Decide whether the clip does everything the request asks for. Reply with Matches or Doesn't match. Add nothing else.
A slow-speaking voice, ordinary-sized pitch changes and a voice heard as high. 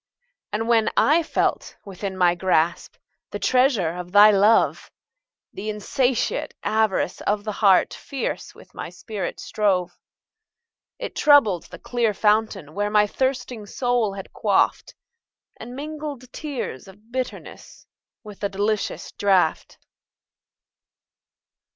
Matches